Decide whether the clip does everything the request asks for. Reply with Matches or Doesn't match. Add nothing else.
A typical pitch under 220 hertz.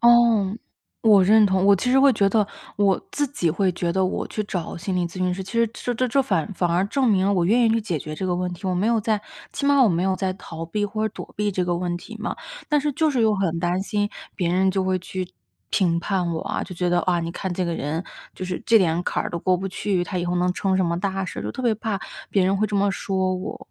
Matches